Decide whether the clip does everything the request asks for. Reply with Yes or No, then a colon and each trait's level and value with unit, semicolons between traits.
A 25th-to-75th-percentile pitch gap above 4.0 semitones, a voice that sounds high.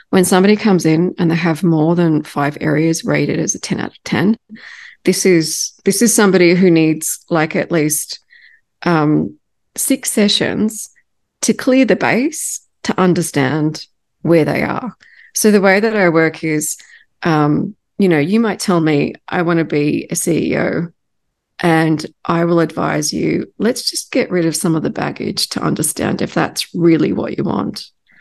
No: average, 5.1 semitones; medium, 175 Hz